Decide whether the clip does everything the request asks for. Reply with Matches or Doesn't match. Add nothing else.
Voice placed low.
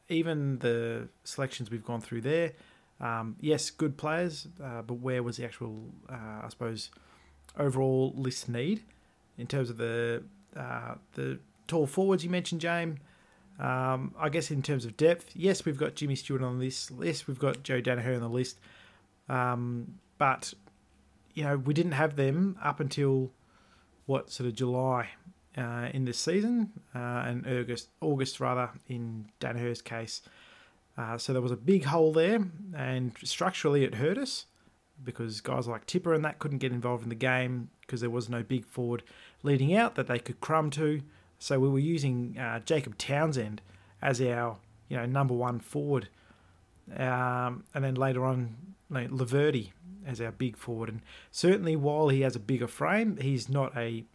Matches